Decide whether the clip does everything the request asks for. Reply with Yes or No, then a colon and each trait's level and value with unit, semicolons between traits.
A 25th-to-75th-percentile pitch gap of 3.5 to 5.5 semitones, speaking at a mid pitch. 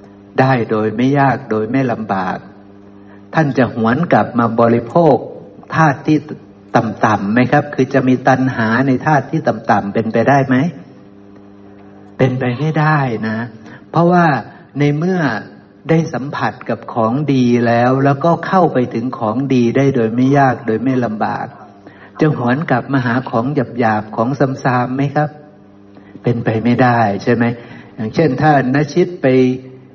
No: average, 4.0 semitones; low, 125 Hz